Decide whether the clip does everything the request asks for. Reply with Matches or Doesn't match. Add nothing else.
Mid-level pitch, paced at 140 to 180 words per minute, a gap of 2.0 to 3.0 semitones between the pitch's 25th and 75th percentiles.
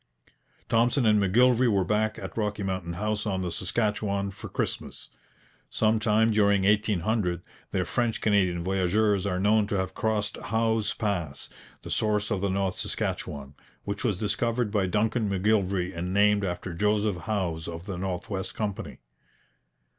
Doesn't match